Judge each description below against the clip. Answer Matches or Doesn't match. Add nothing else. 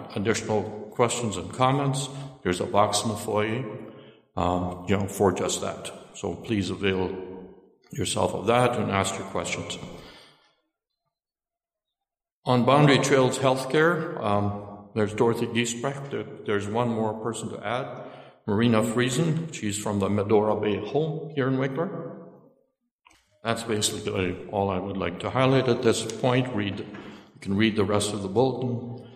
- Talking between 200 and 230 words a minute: Doesn't match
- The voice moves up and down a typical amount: Matches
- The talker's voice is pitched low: Matches